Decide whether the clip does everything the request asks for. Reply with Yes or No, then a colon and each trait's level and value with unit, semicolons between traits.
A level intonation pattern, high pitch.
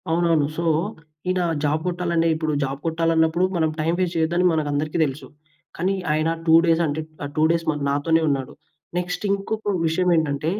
No: narrow, 2.0 semitones; medium, 160 Hz